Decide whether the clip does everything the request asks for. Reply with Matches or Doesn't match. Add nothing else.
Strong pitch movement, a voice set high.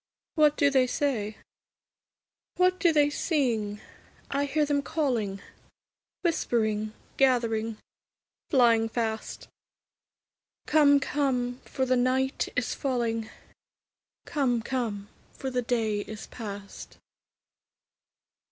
Doesn't match